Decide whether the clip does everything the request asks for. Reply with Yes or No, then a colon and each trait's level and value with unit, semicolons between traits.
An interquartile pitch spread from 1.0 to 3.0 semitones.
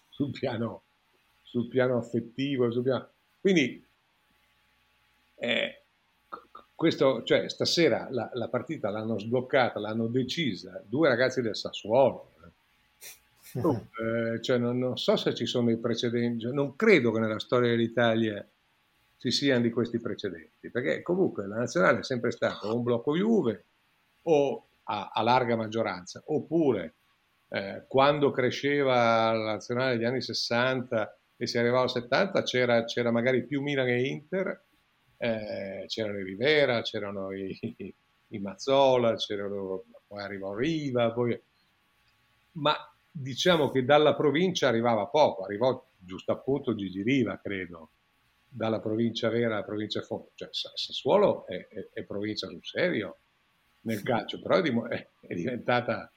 Yes: narrow, 2.6 semitones